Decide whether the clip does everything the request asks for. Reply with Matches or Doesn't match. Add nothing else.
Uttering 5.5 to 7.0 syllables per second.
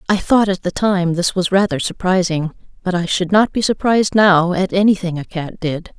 Doesn't match